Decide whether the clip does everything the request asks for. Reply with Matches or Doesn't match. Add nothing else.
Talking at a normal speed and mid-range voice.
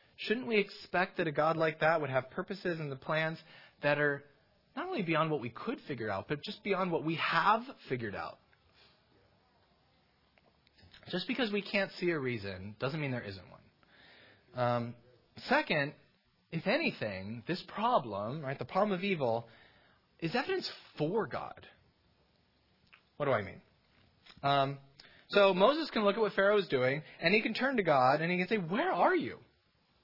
Matches